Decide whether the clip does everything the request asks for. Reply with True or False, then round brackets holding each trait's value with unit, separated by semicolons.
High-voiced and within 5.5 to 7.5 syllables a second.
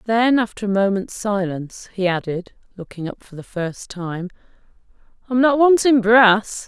False (205 Hz; 4.6 syllables/s)